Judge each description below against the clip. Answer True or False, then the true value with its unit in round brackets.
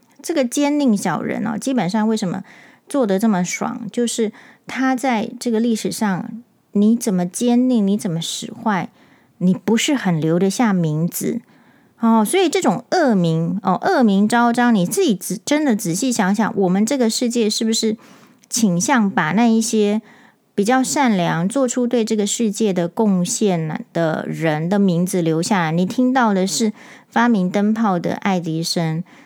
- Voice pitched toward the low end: False (220 Hz)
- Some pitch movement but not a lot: True (4.3 semitones)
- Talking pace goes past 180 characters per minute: True (240 characters per minute)